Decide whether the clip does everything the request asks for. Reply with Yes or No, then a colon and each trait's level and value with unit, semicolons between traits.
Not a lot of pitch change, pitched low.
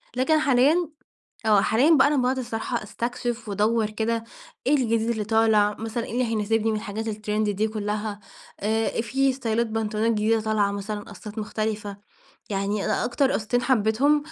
No: narrow, 2.3 semitones; high, 220 Hz